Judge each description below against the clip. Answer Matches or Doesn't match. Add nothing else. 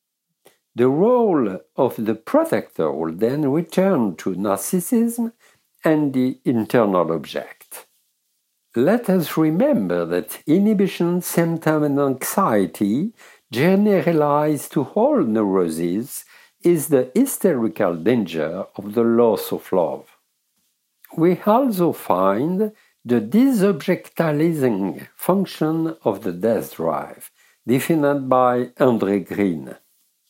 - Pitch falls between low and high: Matches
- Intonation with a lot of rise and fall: Matches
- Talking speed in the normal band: Doesn't match